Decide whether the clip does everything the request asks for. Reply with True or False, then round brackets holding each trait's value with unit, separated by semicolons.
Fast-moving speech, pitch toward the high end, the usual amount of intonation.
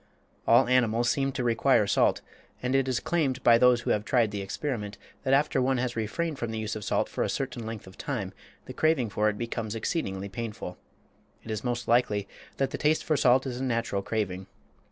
False (215 wpm; 120 Hz; 3.6 semitones)